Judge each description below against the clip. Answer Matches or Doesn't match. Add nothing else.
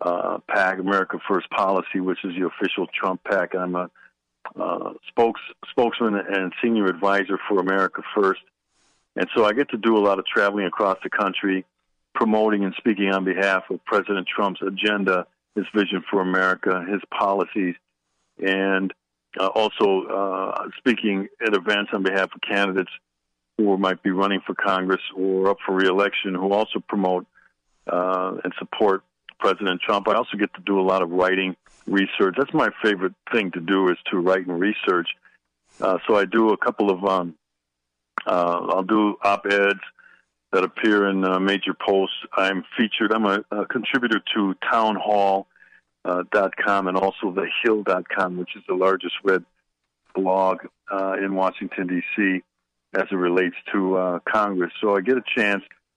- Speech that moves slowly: Doesn't match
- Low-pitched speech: Matches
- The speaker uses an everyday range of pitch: Doesn't match